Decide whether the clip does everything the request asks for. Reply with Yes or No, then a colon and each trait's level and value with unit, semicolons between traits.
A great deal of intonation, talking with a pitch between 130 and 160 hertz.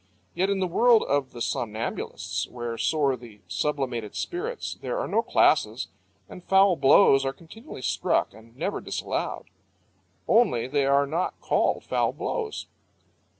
Yes: wide, 8.1 semitones; medium, 140 Hz